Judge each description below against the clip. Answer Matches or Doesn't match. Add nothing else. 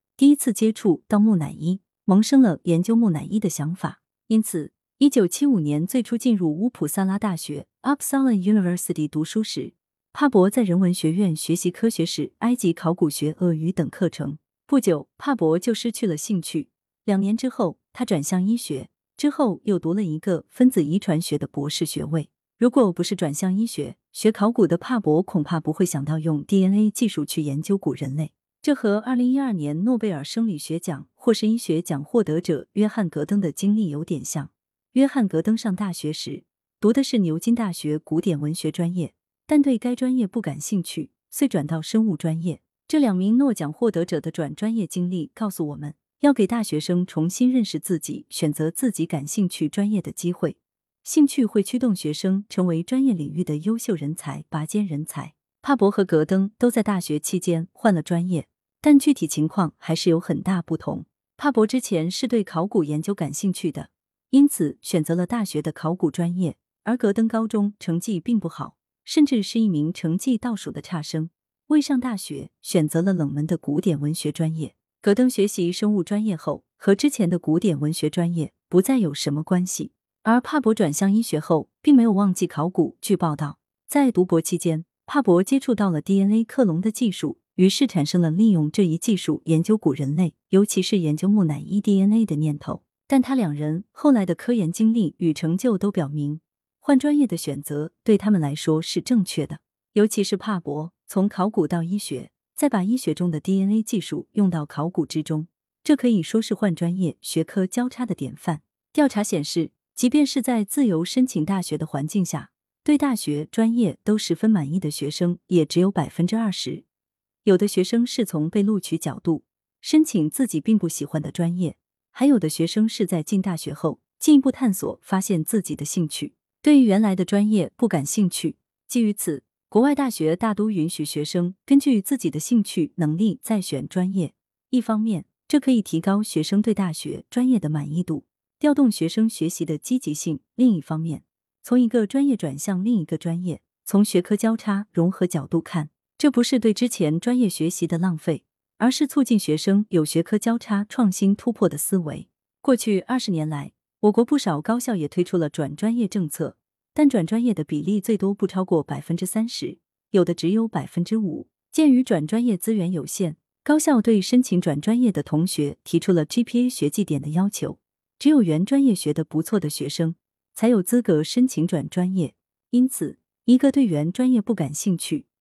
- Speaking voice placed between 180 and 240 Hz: Matches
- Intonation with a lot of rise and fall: Matches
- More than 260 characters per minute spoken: Matches